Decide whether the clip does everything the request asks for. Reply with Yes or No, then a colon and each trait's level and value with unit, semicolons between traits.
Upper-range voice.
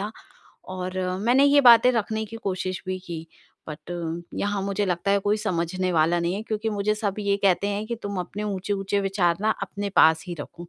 Yes: high, 200 Hz